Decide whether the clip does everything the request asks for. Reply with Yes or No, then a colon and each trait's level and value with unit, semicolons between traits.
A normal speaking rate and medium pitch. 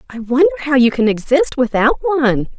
No: average, 185 wpm; very high, 260 Hz